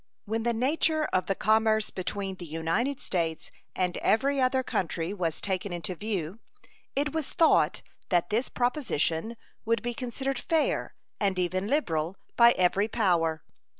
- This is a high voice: Yes, high, 205 Hz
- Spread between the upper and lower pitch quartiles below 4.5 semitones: No, wide, 5.6 semitones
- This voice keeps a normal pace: Yes, average, 150 wpm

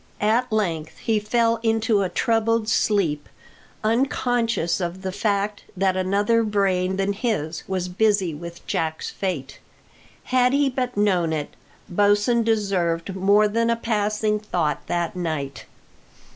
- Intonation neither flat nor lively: Yes, average, 3.9 semitones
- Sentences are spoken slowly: Yes, slow, 130 wpm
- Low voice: No, high, 205 Hz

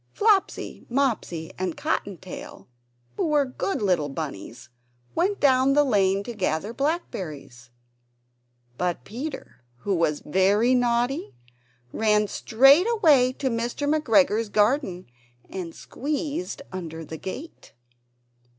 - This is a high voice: Yes, high, 220 Hz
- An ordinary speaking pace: No, slow, 115 wpm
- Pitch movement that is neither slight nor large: No, wide, 7.6 semitones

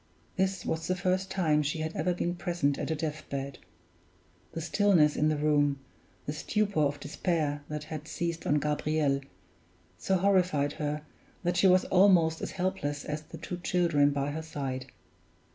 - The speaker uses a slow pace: No, average, 170 wpm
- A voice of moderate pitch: Yes, medium, 155 Hz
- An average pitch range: Yes, average, 3.3 semitones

